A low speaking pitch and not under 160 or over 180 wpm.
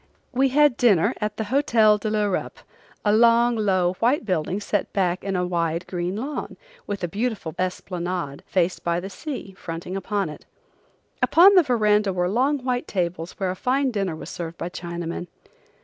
No: high, 195 Hz; average, 170 wpm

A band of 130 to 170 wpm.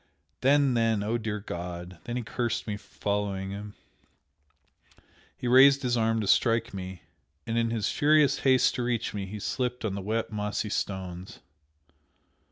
Yes: average, 165 wpm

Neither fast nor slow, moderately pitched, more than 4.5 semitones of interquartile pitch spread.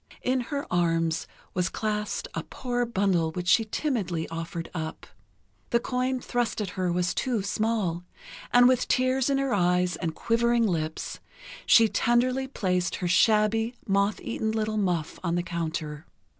No: average, 155 wpm; high, 205 Hz; wide, 5.4 semitones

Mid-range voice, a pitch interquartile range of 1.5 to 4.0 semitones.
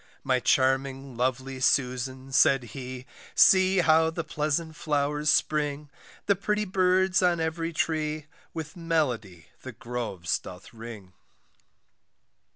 No: medium, 145 Hz; average, 4.4 semitones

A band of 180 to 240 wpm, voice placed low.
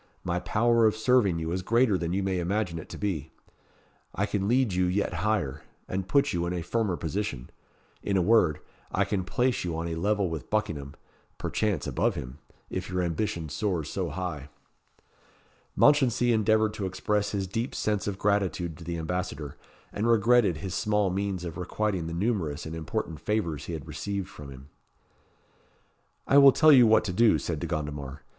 Yes: average, 185 wpm; very low, 95 Hz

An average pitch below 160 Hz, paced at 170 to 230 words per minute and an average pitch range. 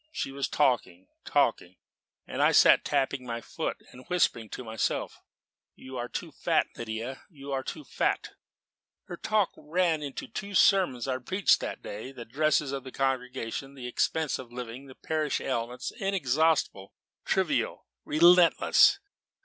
No: low, 135 Hz; average, 155 wpm; average, 4.3 semitones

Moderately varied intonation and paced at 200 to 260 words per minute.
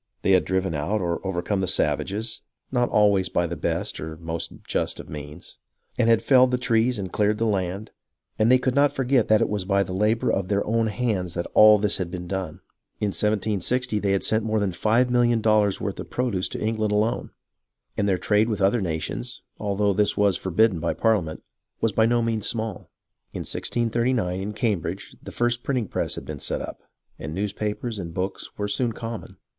Yes: average, 3.3 semitones; fast, 205 wpm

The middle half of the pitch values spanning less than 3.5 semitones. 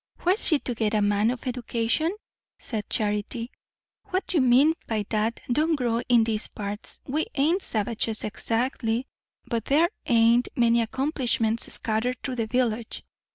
Yes: average, 2.9 semitones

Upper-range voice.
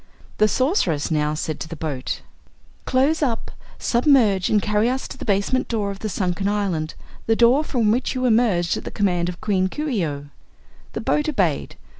Yes: high, 205 Hz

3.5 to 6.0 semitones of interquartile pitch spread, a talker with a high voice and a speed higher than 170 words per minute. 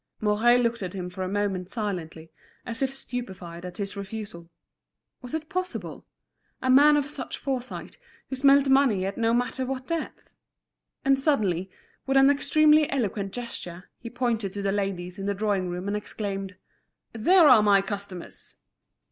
No: wide, 5.6 semitones; high, 215 Hz; average, 160 wpm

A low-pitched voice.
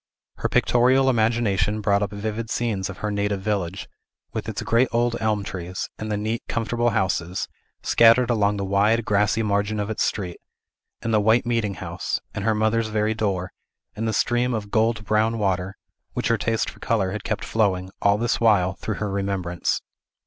Yes: low, 105 Hz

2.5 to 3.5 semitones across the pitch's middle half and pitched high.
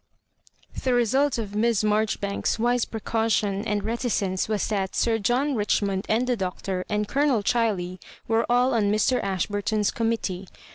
Yes: average, 2.8 semitones; high, 215 Hz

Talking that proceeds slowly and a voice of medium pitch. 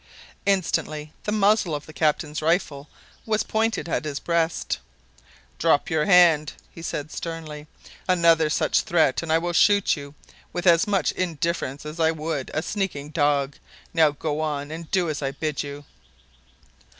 No: average, 160 wpm; medium, 160 Hz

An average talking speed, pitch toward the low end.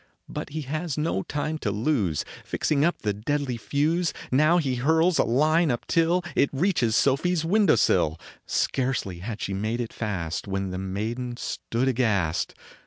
Yes: average, 170 wpm; low, 130 Hz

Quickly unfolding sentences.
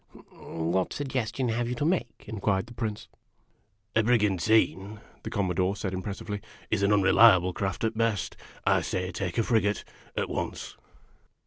No: average, 165 wpm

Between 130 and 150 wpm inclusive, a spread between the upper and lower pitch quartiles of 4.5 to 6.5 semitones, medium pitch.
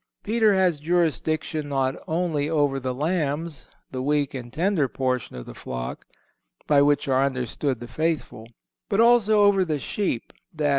Yes: average, 145 wpm; average, 4.8 semitones; medium, 150 Hz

